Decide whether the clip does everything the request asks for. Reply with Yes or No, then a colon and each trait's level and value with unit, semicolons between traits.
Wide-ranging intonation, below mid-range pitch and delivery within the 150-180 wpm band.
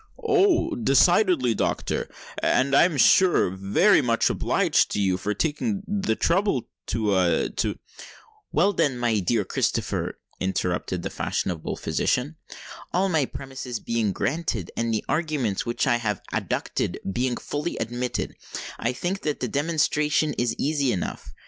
No: wide, 7.1 semitones; low, 130 Hz; average, 140 wpm